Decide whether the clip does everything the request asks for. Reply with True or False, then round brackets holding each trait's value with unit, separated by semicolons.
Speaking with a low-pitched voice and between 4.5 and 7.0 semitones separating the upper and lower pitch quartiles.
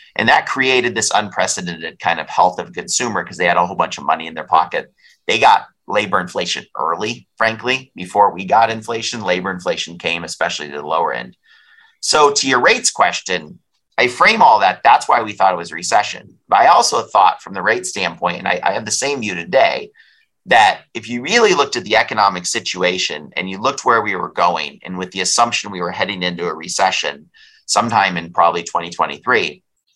True (95 Hz; 4.9 semitones)